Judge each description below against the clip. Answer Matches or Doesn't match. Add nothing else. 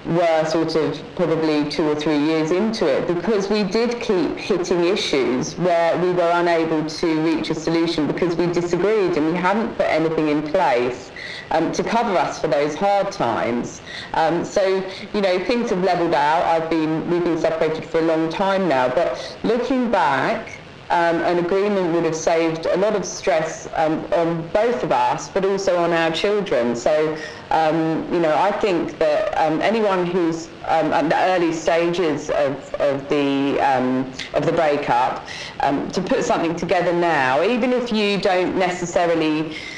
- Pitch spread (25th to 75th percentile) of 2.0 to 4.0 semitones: Matches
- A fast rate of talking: Doesn't match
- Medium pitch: Matches